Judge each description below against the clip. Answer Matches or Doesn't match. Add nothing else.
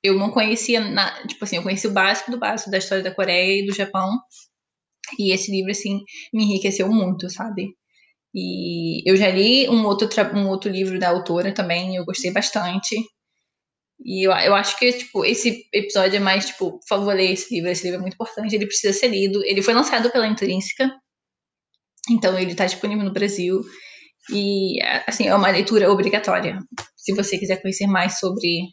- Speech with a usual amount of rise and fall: Doesn't match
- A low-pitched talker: Doesn't match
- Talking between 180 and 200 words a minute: Matches